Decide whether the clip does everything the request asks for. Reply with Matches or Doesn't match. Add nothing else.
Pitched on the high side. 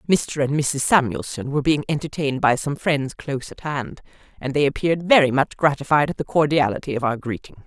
Doesn't match